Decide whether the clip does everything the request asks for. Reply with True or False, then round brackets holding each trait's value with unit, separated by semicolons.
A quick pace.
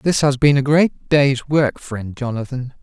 False (190 wpm)